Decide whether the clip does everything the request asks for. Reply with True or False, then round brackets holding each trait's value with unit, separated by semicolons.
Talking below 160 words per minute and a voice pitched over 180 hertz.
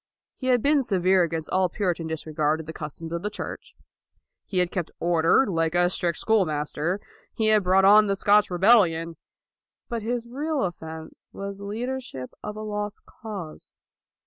False (170 wpm; 190 Hz)